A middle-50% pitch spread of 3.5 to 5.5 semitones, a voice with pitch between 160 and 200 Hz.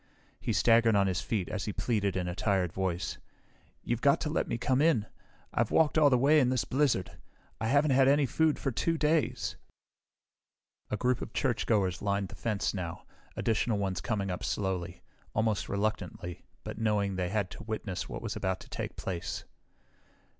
No: average, 5.2 semitones; low, 110 Hz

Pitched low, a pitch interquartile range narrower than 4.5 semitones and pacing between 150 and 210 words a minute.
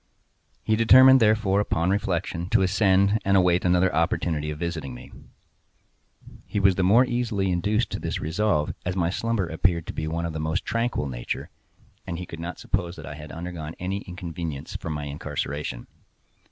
Yes: very low, 90 Hz; average, 3.6 semitones; average, 175 wpm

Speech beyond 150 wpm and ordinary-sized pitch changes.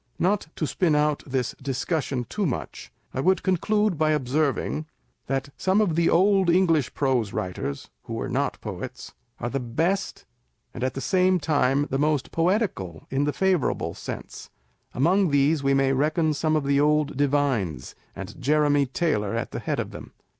Yes: average, 175 wpm; average, 4.1 semitones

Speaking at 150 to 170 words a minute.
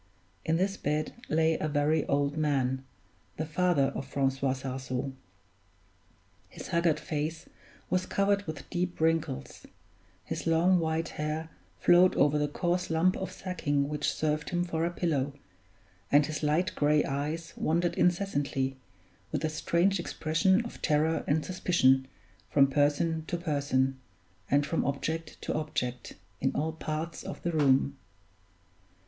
No: average, 140 wpm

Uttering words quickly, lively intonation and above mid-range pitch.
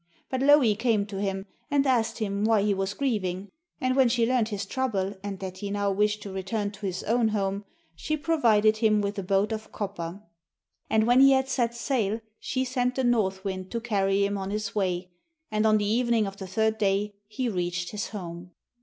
No: fast, 210 wpm; average, 3.2 semitones; high, 210 Hz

